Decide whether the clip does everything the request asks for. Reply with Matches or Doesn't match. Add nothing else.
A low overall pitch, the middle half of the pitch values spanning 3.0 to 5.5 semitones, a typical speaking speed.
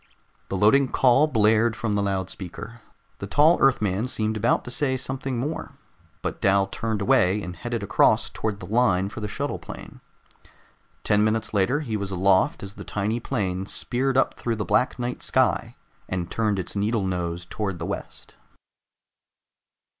Matches